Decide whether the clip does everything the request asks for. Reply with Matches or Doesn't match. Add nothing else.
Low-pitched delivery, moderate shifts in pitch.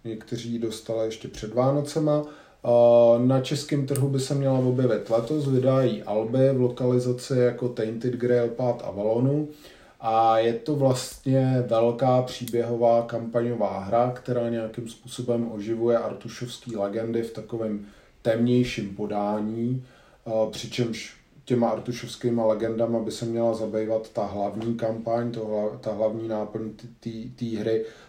Doesn't match